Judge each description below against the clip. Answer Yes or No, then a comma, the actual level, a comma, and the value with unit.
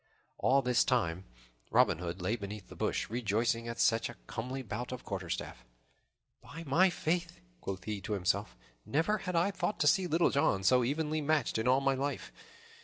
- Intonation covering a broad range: Yes, wide, 6.7 semitones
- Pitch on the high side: No, low, 125 Hz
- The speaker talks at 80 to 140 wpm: No, average, 180 wpm